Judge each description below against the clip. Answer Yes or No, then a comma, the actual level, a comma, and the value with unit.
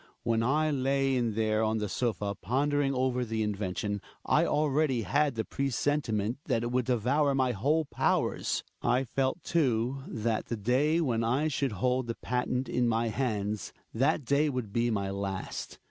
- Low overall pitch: Yes, low, 125 Hz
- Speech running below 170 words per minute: No, average, 175 wpm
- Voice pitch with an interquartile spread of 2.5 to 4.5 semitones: Yes, average, 3.7 semitones